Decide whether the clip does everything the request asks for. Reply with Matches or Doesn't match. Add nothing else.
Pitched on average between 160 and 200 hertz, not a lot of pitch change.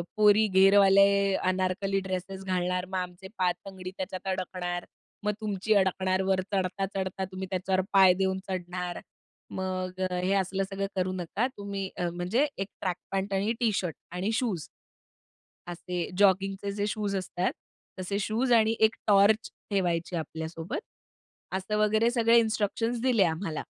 Matches